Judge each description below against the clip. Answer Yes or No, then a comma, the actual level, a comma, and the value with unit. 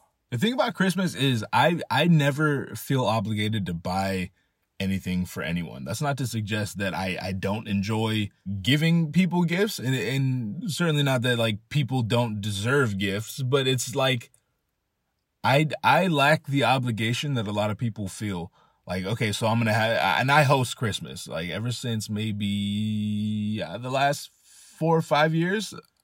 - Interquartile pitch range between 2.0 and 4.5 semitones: No, wide, 5.4 semitones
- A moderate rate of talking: Yes, average, 165 wpm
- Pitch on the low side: Yes, low, 120 Hz